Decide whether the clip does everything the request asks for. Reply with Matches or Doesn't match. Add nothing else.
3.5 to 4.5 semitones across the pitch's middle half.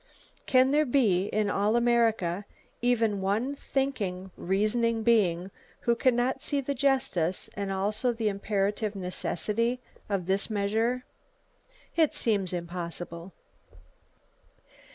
Matches